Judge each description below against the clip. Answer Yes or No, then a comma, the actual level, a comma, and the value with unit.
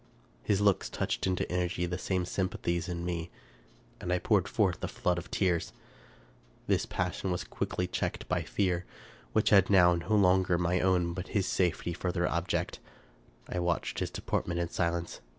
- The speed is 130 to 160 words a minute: No, average, 170 wpm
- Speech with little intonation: Yes, narrow, 1.5 semitones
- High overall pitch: No, very low, 90 Hz